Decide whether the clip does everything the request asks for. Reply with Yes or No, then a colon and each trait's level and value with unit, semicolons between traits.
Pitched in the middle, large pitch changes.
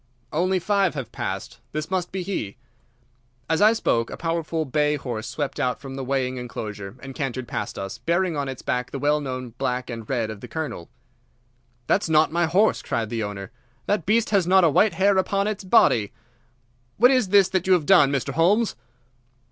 Yes: medium, 150 Hz; wide, 7.0 semitones